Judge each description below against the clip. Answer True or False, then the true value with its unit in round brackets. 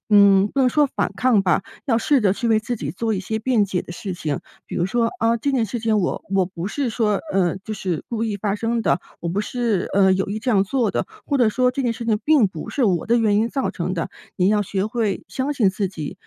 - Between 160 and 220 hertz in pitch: True (215 Hz)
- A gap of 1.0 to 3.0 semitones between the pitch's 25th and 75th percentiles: False (3.6 semitones)